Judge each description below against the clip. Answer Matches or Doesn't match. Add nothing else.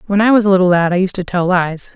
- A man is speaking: Doesn't match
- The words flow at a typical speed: Doesn't match